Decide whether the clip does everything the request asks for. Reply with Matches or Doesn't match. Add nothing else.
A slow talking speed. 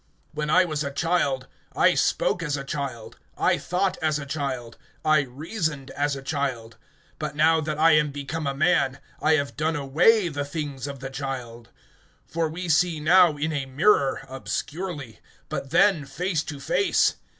Doesn't match